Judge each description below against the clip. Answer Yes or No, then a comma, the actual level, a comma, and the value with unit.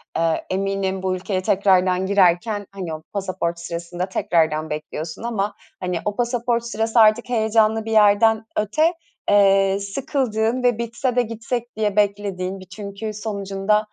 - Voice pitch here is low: No, high, 205 Hz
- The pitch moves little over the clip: No, average, 3.0 semitones